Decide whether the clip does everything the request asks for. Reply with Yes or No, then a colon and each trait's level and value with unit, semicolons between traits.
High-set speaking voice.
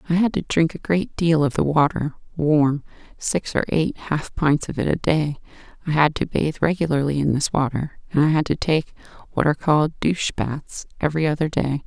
No: medium, 155 Hz